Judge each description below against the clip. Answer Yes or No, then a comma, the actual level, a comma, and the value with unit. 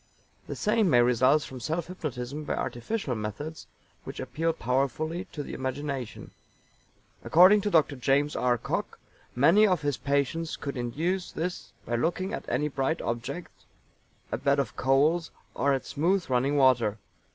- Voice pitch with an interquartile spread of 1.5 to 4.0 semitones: No, average, 4.5 semitones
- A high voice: No, medium, 145 Hz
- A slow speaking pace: No, average, 150 wpm